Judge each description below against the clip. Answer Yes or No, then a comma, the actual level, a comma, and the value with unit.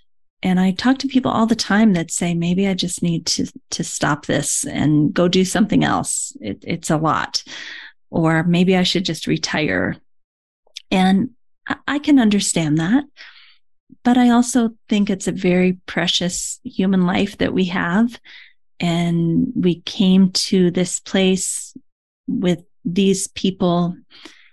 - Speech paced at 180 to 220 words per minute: No, average, 150 wpm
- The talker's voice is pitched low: No, high, 190 Hz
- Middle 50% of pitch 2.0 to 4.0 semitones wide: No, average, 4.5 semitones